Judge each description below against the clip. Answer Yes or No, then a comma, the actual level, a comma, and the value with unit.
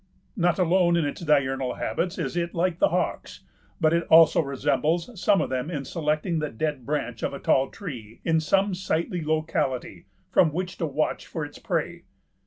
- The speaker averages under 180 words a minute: No, average, 185 wpm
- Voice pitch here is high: No, medium, 160 Hz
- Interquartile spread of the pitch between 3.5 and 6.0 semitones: Yes, average, 3.8 semitones